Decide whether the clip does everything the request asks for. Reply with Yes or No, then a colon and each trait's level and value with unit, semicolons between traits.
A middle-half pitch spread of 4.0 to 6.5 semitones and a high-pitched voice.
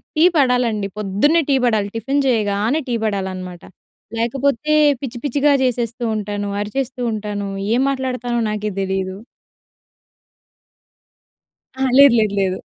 Yes: average, 4.5 semitones; high, 230 Hz